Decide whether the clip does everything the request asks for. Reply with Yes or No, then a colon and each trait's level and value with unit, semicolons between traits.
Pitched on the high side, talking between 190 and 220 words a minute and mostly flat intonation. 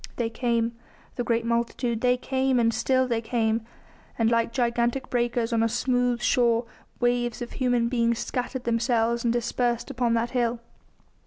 No: high, 235 Hz; average, 160 wpm; narrow, 1.1 semitones